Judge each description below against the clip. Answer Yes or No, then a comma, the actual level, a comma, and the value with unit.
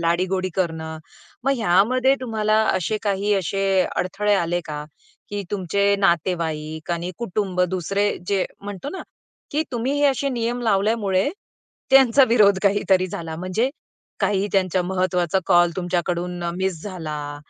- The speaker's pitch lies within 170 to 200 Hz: Yes, high, 190 Hz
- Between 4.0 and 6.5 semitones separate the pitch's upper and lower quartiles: No, average, 3.2 semitones